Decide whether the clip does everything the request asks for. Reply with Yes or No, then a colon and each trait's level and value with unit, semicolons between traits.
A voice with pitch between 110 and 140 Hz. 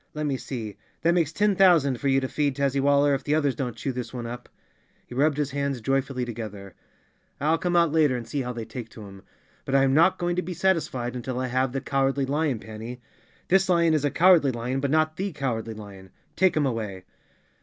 Yes: low, 135 Hz